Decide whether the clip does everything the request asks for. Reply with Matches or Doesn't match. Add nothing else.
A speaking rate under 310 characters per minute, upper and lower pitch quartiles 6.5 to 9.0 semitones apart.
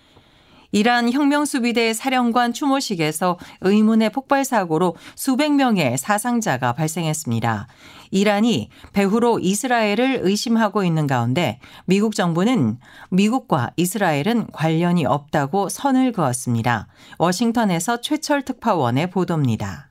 Matches